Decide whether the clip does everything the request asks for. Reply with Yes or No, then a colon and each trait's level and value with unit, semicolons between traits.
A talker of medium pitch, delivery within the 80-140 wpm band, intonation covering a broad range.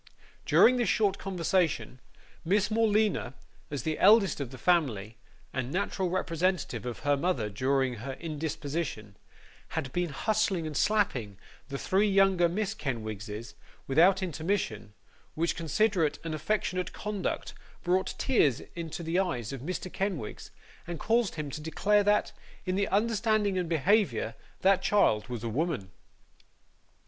Yes: medium, 170 Hz; slow, 135 wpm; wide, 6.5 semitones